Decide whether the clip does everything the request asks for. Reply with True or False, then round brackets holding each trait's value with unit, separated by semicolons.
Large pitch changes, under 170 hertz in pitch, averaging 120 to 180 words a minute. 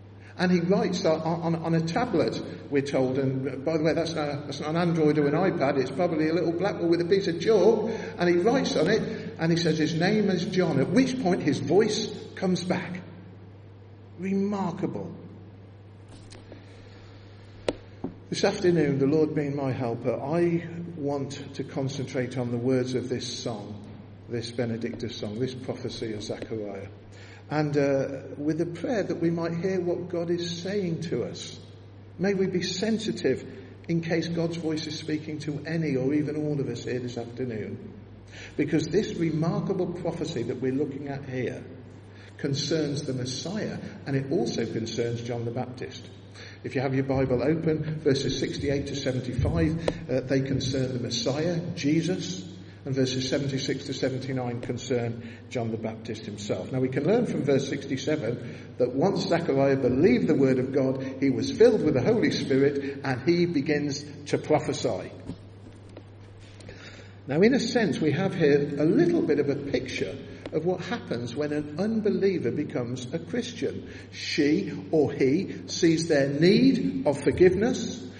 True (5.8 semitones; 140 Hz; 165 wpm)